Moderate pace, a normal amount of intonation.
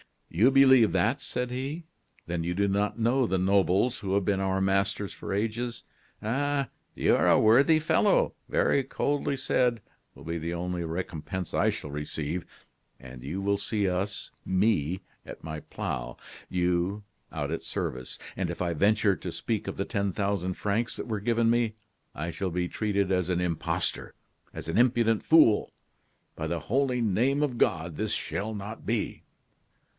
Yes: average, 170 wpm; average, 4.8 semitones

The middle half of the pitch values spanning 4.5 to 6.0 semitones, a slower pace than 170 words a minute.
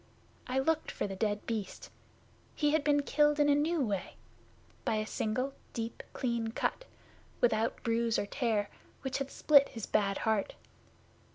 Yes: average, 4.9 semitones; average, 160 wpm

